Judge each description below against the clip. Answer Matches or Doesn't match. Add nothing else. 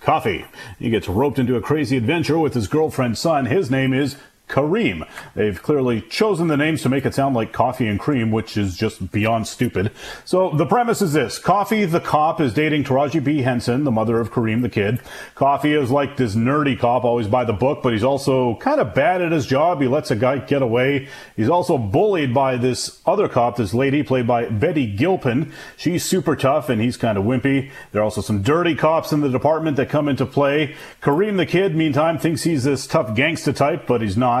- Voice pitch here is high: Doesn't match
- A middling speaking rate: Doesn't match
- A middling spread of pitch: Matches